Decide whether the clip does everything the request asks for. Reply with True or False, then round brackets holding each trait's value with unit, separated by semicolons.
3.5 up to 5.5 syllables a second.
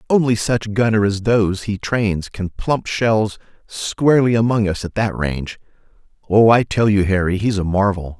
True (4.7 syllables/s)